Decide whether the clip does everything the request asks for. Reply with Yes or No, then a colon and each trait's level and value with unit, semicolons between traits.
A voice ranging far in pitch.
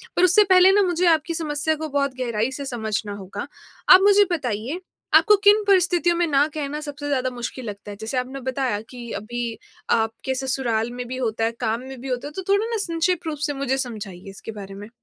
Yes: wide, 6.3 semitones